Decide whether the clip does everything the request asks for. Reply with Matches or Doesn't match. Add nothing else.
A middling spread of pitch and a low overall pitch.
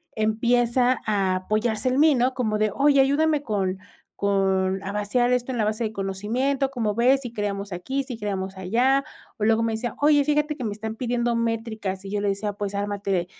Doesn't match